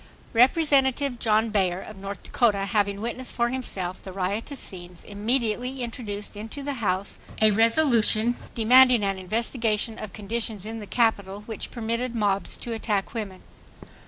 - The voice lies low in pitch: No, high, 220 Hz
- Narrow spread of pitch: No, average, 3.1 semitones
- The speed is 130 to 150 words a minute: Yes, average, 145 wpm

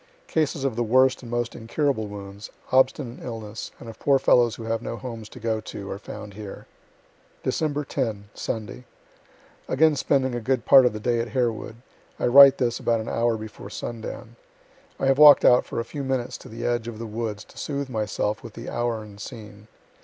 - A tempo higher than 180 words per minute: Yes, average, 200 wpm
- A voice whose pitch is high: No, low, 115 Hz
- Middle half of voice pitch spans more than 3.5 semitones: No, average, 3.1 semitones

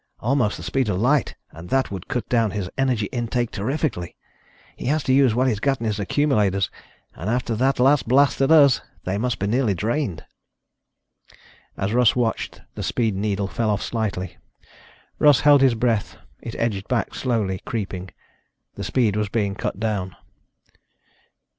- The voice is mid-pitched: No, low, 115 Hz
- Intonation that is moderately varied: Yes, average, 4.3 semitones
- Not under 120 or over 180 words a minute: Yes, average, 165 wpm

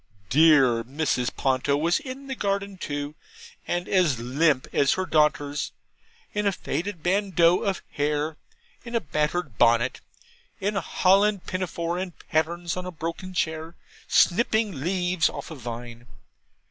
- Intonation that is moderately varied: Yes, average, 4.5 semitones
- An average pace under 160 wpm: Yes, average, 140 wpm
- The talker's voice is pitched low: No, medium, 165 Hz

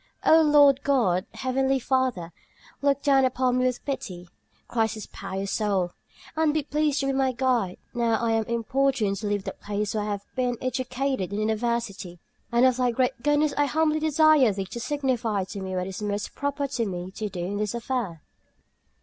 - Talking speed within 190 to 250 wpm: Yes, average, 195 wpm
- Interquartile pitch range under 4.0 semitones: No, average, 4.9 semitones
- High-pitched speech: Yes, high, 240 Hz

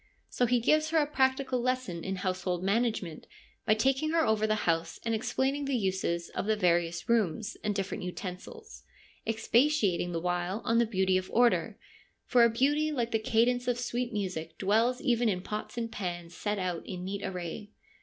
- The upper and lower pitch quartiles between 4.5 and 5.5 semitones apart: Yes, average, 5.1 semitones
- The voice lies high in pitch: Yes, high, 220 Hz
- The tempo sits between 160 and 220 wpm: Yes, average, 190 wpm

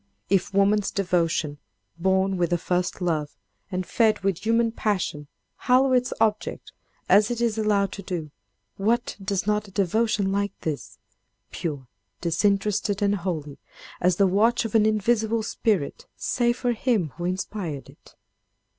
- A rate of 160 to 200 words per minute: No, average, 140 wpm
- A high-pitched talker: Yes, high, 200 Hz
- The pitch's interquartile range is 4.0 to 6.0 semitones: No, average, 3.5 semitones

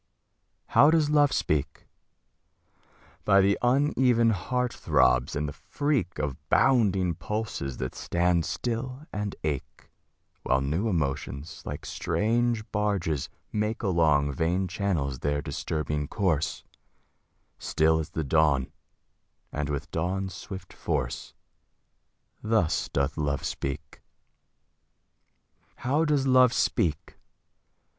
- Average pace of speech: No, slow, 110 wpm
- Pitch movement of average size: No, wide, 7.4 semitones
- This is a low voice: Yes, very low, 90 Hz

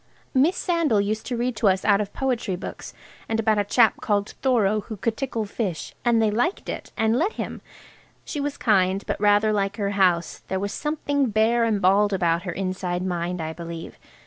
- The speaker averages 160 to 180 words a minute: No, average, 200 wpm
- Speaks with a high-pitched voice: Yes, high, 210 Hz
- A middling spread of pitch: Yes, average, 3.7 semitones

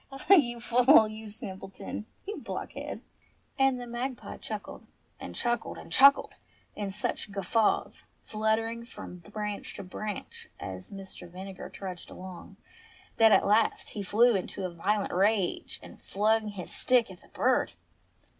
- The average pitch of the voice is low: No, high, 215 Hz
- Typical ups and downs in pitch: Yes, average, 3.6 semitones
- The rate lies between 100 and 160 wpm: Yes, average, 145 wpm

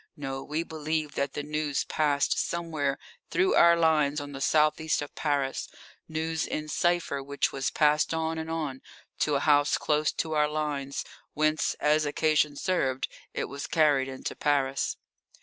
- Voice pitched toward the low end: No, medium, 150 Hz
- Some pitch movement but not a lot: No, narrow, 1.9 semitones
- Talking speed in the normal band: Yes, average, 165 wpm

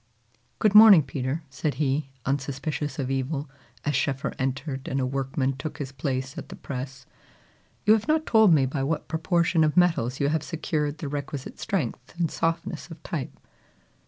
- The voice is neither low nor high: Yes, medium, 145 Hz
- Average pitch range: Yes, average, 3.5 semitones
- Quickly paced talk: No, average, 170 wpm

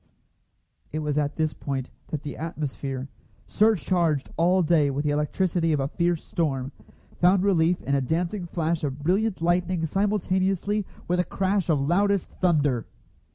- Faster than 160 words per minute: No, average, 155 wpm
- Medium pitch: Yes, medium, 165 Hz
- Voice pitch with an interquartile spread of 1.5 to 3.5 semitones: No, average, 4.0 semitones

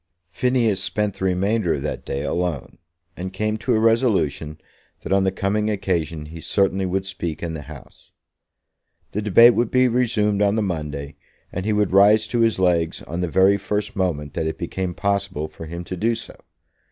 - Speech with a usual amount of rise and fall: Yes, average, 4.0 semitones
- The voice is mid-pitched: No, very low, 95 Hz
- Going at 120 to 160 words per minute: No, average, 190 wpm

